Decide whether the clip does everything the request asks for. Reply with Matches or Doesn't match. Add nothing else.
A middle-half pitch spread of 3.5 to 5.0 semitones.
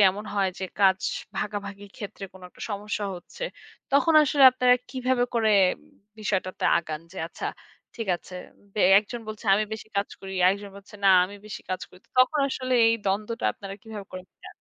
Doesn't match